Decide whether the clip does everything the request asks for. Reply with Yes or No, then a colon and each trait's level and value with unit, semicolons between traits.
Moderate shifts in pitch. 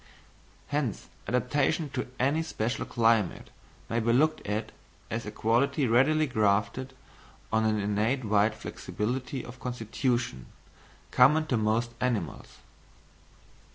Yes: average, 3.5 semitones